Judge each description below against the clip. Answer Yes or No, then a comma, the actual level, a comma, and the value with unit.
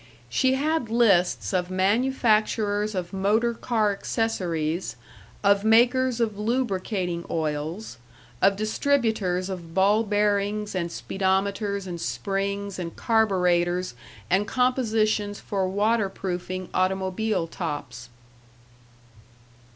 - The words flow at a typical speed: No, slow, 95 wpm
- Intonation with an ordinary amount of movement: Yes, average, 3.3 semitones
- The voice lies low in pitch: No, high, 200 Hz